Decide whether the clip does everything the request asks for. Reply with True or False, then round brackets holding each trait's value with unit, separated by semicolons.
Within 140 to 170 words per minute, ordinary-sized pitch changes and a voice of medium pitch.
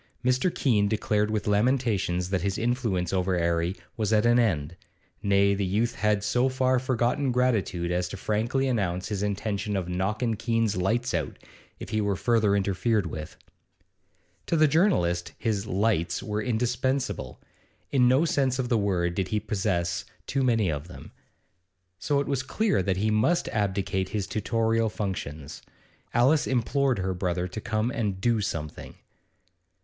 False (160 wpm; 4.4 semitones; 105 Hz)